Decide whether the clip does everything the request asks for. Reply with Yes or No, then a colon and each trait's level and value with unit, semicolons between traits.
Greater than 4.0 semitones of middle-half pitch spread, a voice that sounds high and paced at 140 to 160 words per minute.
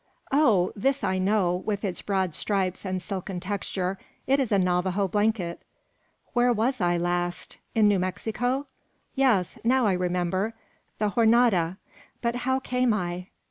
Yes: average, 4.5 semitones; high, 200 Hz; average, 145 wpm